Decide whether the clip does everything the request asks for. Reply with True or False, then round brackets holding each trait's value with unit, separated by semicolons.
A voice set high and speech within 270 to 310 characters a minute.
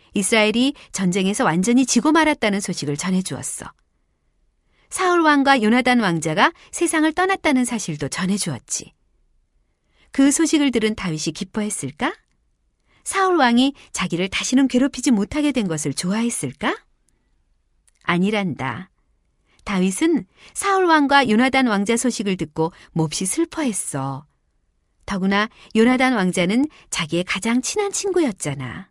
True (215 Hz; 285 characters per minute)